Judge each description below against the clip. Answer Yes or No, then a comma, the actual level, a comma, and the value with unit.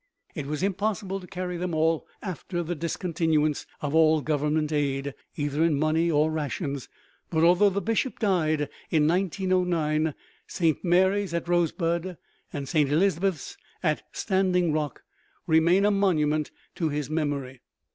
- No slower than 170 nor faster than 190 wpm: No, average, 140 wpm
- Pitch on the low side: No, medium, 160 Hz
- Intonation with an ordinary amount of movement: Yes, average, 3.2 semitones